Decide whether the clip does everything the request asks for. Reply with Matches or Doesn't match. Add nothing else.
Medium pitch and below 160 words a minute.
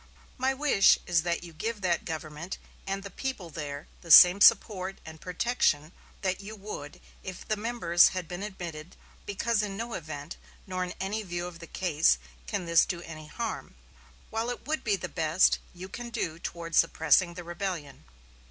Doesn't match